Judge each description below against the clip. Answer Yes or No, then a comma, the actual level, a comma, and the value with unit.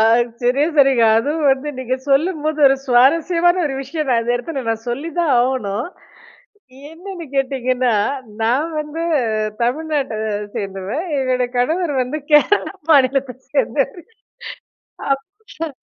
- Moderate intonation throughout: Yes, average, 3.8 semitones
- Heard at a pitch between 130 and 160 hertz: No, very high, 275 Hz